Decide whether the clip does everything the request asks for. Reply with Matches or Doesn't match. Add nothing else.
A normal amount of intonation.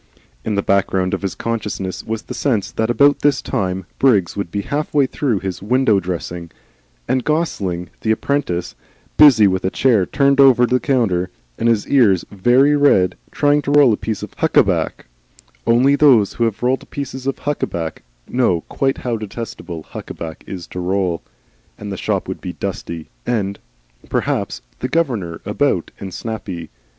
Doesn't match